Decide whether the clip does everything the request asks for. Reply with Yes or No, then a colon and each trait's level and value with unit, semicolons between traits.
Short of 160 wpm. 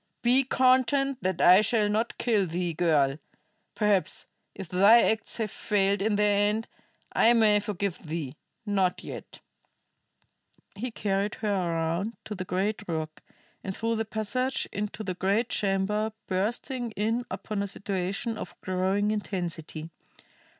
Yes: average, 140 wpm